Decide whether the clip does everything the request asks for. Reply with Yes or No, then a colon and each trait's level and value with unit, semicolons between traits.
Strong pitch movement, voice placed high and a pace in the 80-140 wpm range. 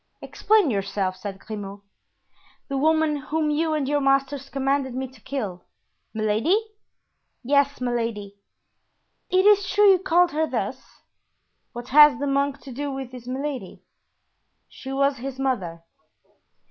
No: average, 4.0 semitones; very high, 275 Hz; slow, 135 wpm